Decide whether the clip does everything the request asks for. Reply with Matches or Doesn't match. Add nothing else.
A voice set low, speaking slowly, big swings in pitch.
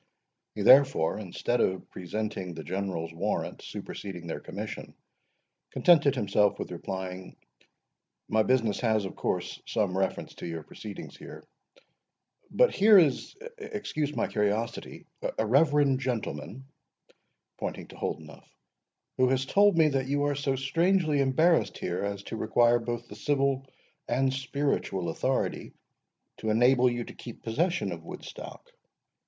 Matches